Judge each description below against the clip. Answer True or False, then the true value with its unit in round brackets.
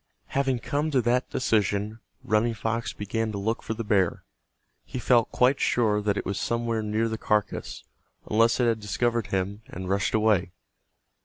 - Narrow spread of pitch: True (2.3 semitones)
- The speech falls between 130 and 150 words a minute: False (170 wpm)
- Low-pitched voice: True (110 Hz)